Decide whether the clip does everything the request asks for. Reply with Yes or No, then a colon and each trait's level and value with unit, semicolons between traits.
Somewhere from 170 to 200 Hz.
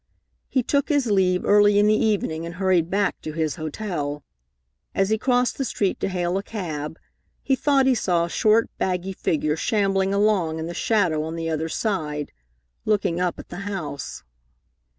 Yes: high, 190 Hz